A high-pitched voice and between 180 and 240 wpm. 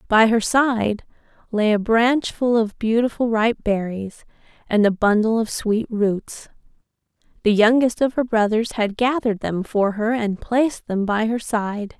No: high, 220 Hz; average, 165 wpm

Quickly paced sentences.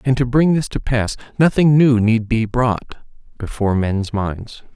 No: average, 175 wpm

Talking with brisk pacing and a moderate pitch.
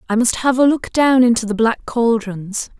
No: fast, 215 wpm; high, 235 Hz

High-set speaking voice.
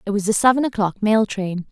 Yes: high, 210 Hz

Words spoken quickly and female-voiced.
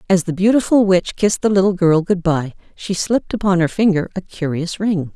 Yes: fast, 210 wpm; female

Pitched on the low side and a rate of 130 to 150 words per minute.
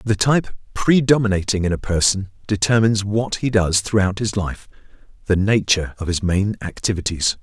Yes: low, 100 Hz; average, 145 wpm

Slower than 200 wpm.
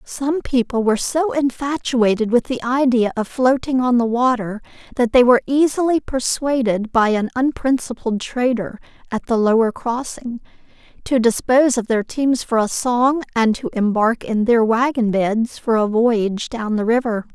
Yes: average, 165 wpm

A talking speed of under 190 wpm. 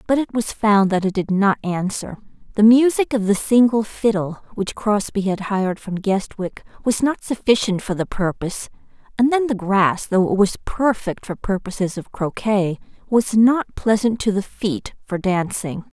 Yes: average, 175 wpm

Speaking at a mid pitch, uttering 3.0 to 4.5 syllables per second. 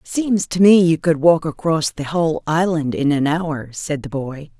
Yes: medium, 160 Hz; 4.3 syllables/s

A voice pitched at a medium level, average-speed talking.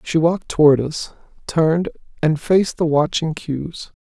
Yes: medium, 155 Hz; average, 150 wpm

